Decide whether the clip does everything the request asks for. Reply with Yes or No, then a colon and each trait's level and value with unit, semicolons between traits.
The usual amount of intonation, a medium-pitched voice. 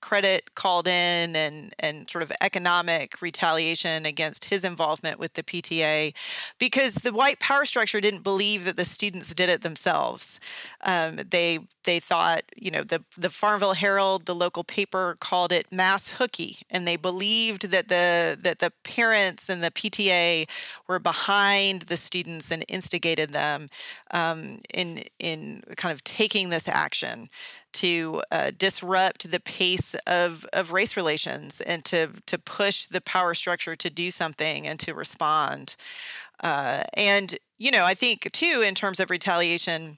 Yes: average, 3.0 semitones; medium, 180 Hz